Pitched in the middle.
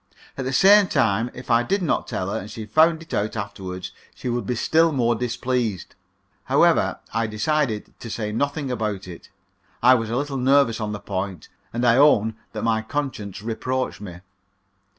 No: low, 115 Hz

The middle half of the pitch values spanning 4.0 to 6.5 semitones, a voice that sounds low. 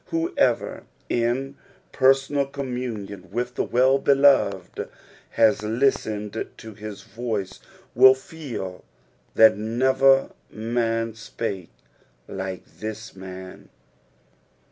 Yes: average, 4.3 semitones; low, 115 Hz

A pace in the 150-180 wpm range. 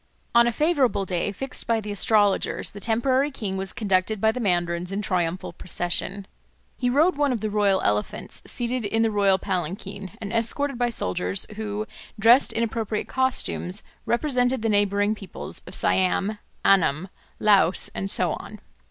Yes: average, 160 wpm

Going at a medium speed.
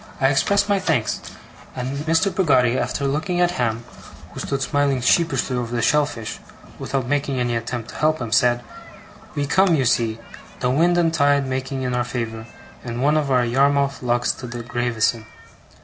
Yes: average, 175 wpm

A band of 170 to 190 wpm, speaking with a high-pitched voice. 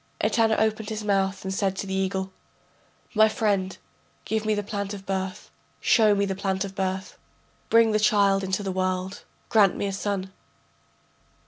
Yes: average, 175 wpm; high, 195 Hz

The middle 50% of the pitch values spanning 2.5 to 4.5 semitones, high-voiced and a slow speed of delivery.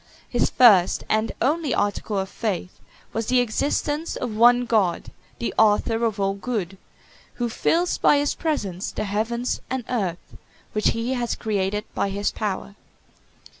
No: average, 3.5 semitones; high, 220 Hz; average, 150 wpm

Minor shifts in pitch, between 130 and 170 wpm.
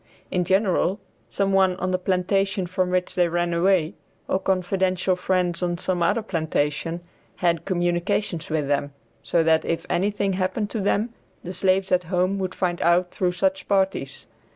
Yes: narrow, 1.8 semitones; average, 165 wpm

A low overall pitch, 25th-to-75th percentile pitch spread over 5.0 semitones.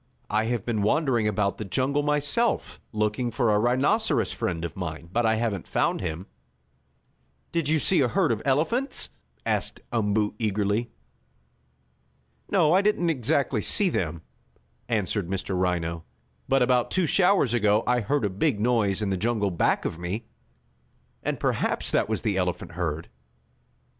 Yes: low, 110 Hz; wide, 5.6 semitones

